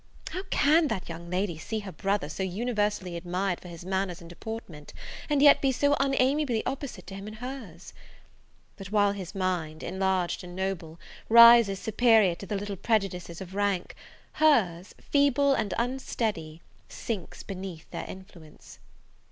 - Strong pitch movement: No, average, 4.7 semitones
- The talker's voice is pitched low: No, high, 195 Hz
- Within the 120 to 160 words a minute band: Yes, average, 150 wpm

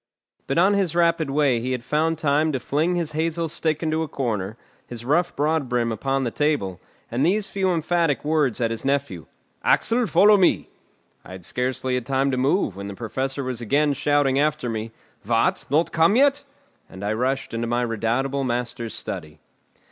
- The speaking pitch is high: No, low, 135 Hz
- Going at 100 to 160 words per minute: No, average, 185 wpm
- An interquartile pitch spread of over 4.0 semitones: Yes, average, 5.1 semitones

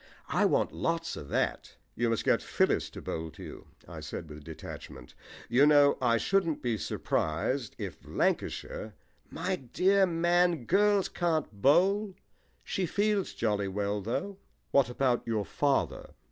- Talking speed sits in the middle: Yes, average, 150 wpm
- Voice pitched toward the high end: No, low, 135 Hz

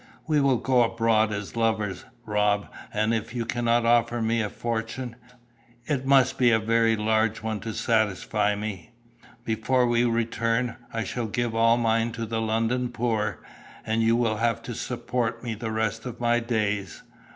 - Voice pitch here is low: Yes, low, 115 Hz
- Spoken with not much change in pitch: Yes, narrow, 1.5 semitones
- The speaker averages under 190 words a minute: Yes, average, 170 wpm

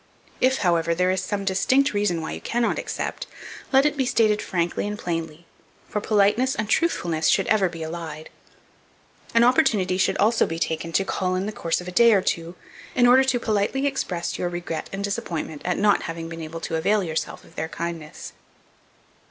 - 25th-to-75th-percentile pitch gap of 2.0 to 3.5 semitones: No, average, 4.7 semitones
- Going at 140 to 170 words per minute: No, average, 195 wpm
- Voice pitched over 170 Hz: Yes, medium, 185 Hz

